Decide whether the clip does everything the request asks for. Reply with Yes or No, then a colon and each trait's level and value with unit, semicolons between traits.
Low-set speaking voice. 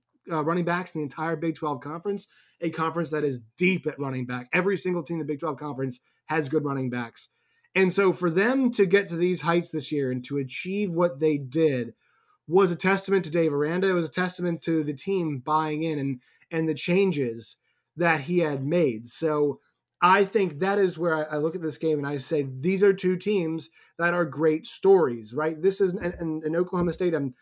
No: medium, 165 Hz